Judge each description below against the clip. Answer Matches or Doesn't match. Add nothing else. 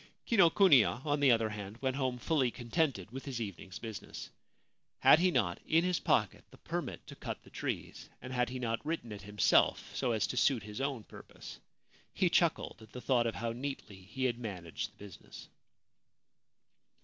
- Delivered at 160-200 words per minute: Matches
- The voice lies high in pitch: Doesn't match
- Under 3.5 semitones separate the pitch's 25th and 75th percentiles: Doesn't match